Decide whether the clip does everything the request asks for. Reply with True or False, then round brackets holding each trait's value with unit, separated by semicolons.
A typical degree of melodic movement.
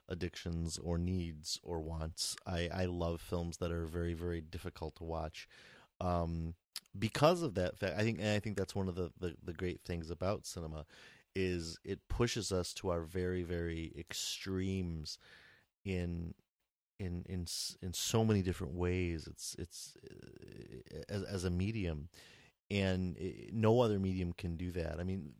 False (2.1 semitones)